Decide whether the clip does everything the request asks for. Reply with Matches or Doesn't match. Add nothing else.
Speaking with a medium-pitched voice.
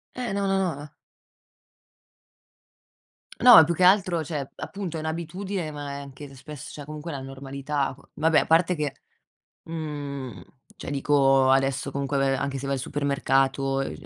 Matches